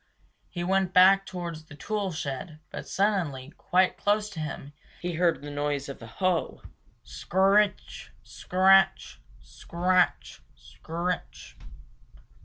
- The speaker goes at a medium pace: No, slow, 125 wpm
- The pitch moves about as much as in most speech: Yes, average, 3.7 semitones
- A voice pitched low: No, medium, 180 Hz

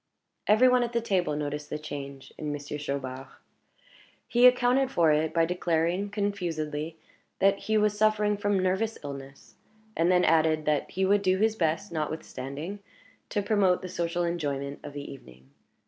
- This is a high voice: No, medium, 170 Hz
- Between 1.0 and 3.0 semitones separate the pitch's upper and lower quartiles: No, wide, 5.5 semitones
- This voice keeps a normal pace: Yes, average, 165 wpm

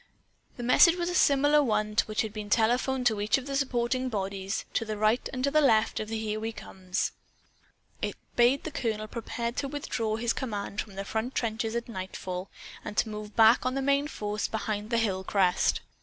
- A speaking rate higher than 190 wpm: Yes, average, 200 wpm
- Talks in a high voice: Yes, high, 225 Hz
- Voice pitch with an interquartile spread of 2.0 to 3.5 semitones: Yes, average, 3.2 semitones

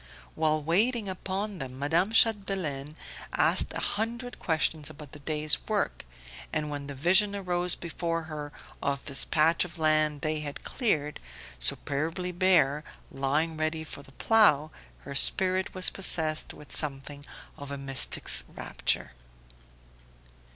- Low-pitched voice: No, medium, 155 Hz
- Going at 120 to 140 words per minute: Yes, slow, 135 wpm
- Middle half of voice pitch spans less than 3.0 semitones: No, average, 4.2 semitones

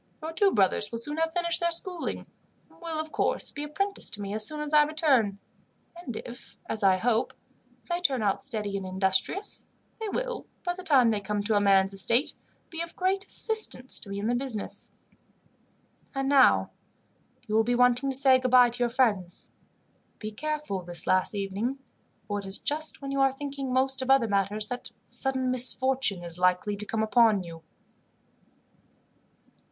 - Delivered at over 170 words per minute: Yes, average, 180 wpm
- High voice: Yes, very high, 250 Hz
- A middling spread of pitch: No, wide, 6.4 semitones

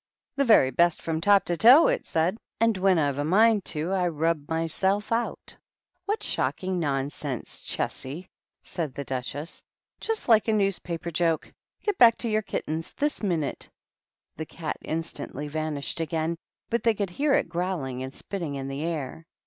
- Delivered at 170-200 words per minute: Yes, average, 175 wpm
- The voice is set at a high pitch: No, medium, 170 Hz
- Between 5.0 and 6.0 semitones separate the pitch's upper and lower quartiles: Yes, average, 5.3 semitones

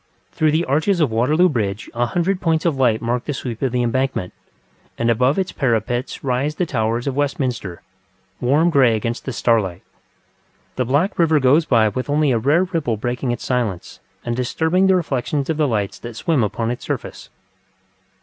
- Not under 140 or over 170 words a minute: No, average, 185 wpm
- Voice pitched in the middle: No, low, 130 Hz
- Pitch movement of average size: Yes, average, 4.7 semitones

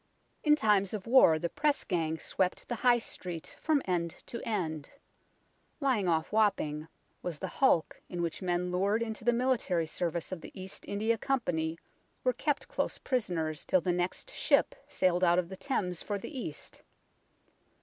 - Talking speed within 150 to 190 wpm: Yes, average, 170 wpm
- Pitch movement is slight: No, wide, 5.4 semitones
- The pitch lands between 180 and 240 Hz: Yes, medium, 185 Hz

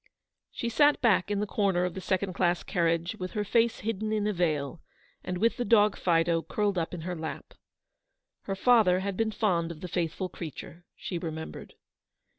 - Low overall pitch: No, medium, 185 Hz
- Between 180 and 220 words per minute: Yes, average, 195 wpm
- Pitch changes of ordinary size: Yes, average, 3.7 semitones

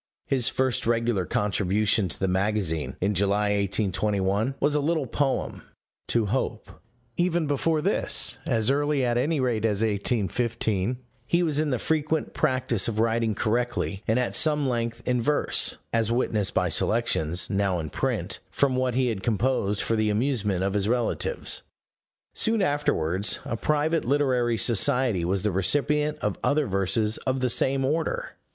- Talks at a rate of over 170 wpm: No, average, 160 wpm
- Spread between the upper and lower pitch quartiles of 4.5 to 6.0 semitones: Yes, average, 5.1 semitones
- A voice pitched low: Yes, low, 115 Hz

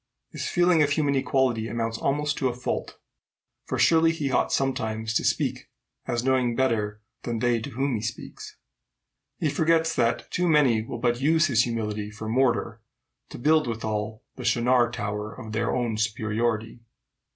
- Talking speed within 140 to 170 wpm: Yes, average, 165 wpm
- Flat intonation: No, average, 3.8 semitones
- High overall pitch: No, low, 120 Hz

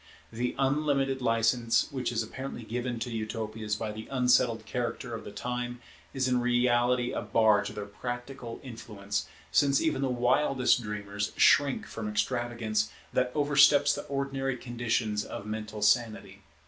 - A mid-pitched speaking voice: No, low, 120 Hz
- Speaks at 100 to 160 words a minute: Yes, average, 145 wpm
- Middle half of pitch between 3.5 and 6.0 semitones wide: No, average, 2.8 semitones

